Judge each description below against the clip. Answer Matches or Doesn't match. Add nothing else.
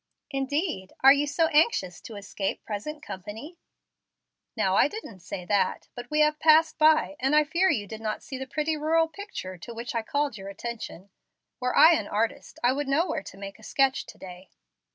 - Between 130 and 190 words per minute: Doesn't match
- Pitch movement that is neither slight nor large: Doesn't match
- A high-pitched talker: Matches